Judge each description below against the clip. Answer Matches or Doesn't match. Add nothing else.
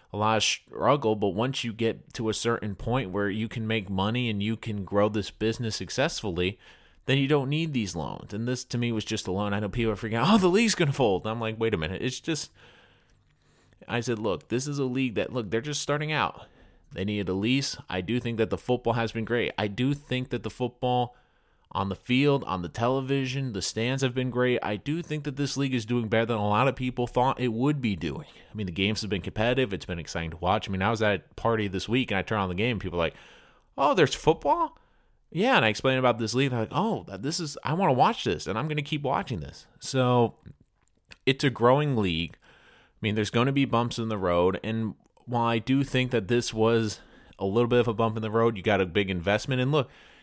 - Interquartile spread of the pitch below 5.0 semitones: Matches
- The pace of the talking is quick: Matches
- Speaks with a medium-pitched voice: Doesn't match